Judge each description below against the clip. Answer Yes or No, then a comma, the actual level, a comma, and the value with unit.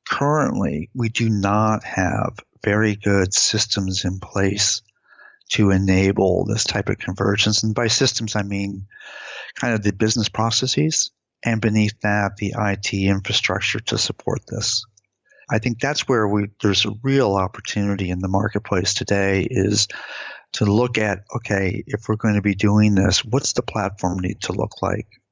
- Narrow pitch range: Yes, narrow, 2.1 semitones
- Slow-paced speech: No, average, 160 wpm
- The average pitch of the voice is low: Yes, low, 105 Hz